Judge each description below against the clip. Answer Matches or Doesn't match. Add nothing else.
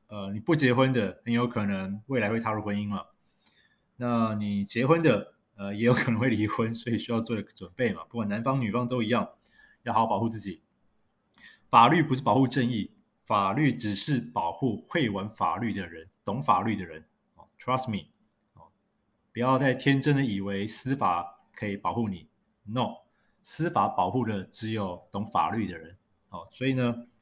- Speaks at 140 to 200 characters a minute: Doesn't match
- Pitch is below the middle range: Matches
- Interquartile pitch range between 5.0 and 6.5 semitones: Doesn't match